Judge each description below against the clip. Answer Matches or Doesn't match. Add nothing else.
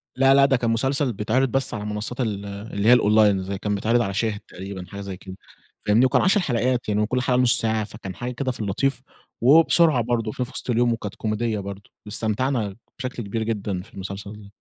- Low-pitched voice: Matches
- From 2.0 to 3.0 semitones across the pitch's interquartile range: Doesn't match